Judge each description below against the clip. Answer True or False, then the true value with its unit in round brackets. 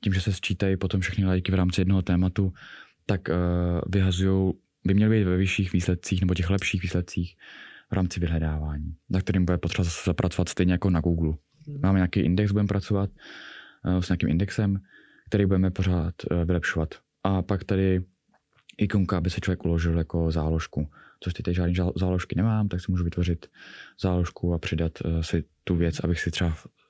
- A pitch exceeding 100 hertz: False (90 Hz)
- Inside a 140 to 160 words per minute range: False (170 wpm)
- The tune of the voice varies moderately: False (1.9 semitones)